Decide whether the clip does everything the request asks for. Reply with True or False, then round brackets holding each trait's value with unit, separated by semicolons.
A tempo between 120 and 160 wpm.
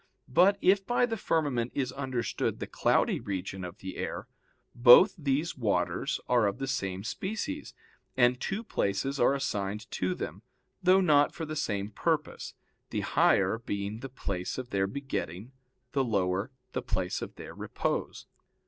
True (155 wpm)